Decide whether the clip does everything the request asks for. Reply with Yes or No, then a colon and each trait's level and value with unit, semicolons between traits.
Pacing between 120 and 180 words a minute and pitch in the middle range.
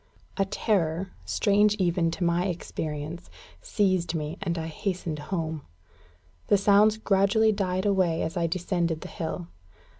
Yes: average, 140 wpm; medium, 180 Hz